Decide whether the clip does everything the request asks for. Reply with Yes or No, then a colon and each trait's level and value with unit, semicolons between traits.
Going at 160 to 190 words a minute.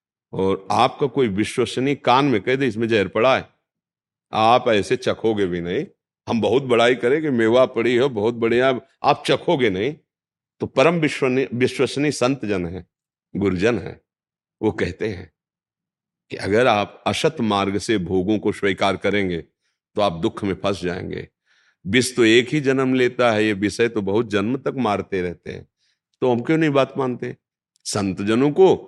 Yes: average, 170 wpm